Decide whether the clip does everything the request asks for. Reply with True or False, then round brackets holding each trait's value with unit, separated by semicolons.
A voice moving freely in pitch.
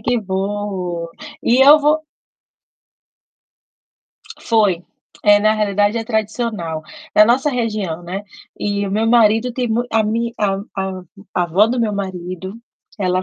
False (3.4 semitones)